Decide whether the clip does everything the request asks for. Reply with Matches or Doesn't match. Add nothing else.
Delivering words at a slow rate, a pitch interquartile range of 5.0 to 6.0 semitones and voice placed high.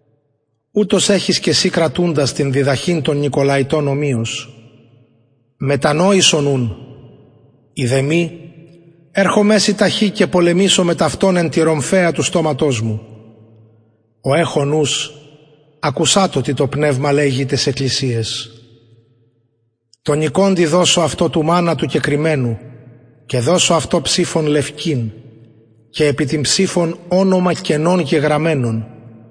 Doesn't match